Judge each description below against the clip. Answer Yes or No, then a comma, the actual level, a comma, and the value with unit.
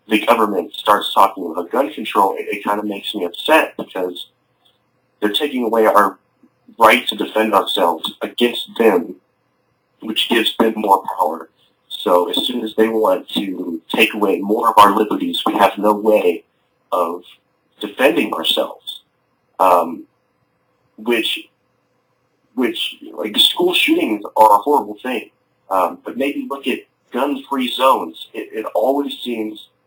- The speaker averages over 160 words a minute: No, average, 140 wpm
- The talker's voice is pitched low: Yes, low, 130 Hz